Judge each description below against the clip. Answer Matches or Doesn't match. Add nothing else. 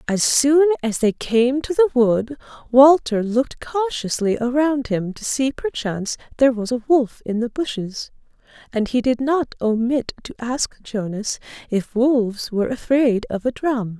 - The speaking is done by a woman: Matches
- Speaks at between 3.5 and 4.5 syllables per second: Matches